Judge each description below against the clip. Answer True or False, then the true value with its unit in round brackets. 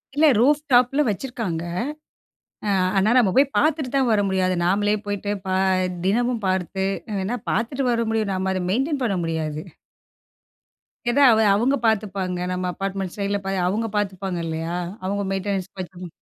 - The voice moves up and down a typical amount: True (4.1 semitones)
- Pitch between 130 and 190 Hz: False (200 Hz)